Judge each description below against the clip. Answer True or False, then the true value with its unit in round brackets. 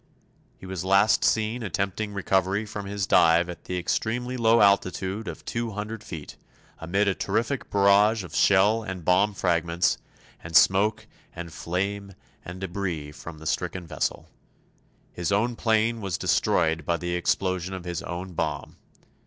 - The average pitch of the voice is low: True (95 Hz)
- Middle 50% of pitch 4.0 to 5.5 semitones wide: False (3.3 semitones)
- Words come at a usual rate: True (155 wpm)